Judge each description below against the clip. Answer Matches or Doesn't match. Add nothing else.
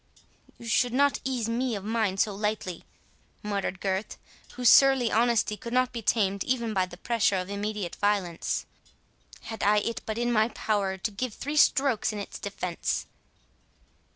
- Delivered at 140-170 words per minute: Matches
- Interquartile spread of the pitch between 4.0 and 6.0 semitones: Doesn't match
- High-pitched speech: Matches